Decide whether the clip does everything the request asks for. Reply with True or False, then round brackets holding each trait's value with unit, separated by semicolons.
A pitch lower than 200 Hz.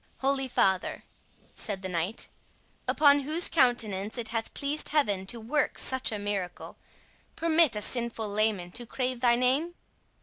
False (235 Hz)